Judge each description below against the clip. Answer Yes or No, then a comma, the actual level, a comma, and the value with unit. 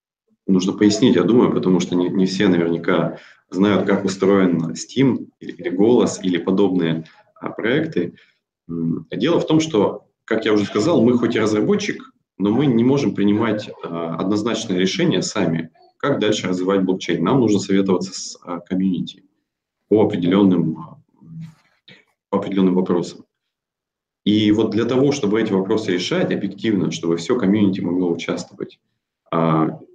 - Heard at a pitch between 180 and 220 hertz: No, very low, 95 Hz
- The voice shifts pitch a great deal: No, average, 3.3 semitones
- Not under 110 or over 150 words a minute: Yes, average, 145 wpm